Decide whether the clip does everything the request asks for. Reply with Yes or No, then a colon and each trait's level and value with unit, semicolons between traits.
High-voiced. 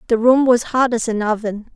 Yes: high, 230 Hz